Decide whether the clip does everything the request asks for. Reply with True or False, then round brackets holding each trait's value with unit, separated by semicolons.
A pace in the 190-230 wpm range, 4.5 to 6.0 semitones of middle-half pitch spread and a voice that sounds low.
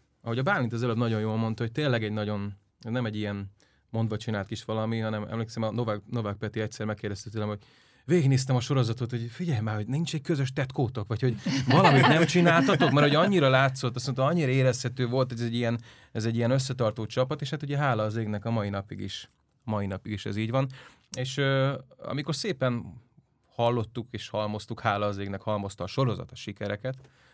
False (200 wpm; 3.7 semitones; 120 Hz)